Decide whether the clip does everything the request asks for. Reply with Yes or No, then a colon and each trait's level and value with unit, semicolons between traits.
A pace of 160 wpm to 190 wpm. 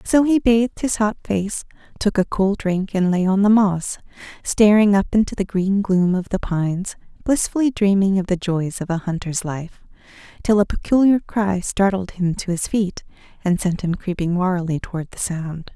Yes: average, 185 wpm